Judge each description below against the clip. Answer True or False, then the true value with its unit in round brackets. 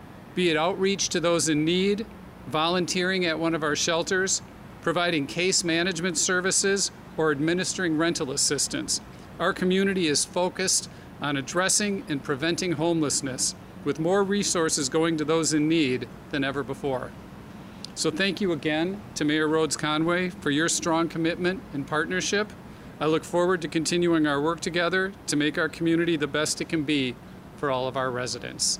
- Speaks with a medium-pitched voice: True (165 Hz)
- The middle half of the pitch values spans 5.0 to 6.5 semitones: False (3.1 semitones)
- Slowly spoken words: False (160 wpm)